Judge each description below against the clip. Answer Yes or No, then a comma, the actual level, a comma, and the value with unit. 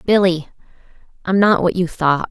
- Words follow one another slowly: Yes, slow, 130 wpm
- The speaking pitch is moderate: Yes, medium, 180 Hz